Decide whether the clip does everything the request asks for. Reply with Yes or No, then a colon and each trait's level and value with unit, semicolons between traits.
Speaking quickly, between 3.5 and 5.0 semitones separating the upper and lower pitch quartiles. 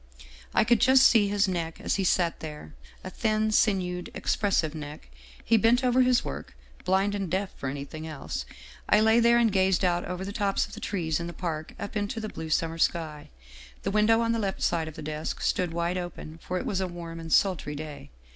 Yes: fast, 220 wpm; average, 4.6 semitones